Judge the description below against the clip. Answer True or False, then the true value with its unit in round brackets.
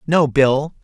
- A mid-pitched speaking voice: True (145 Hz)